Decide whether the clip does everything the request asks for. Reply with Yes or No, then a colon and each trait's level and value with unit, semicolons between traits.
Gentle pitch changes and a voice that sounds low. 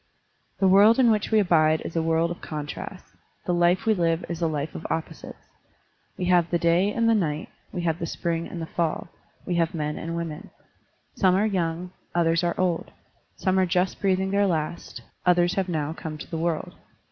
No: narrow, 2.3 semitones; medium, 170 Hz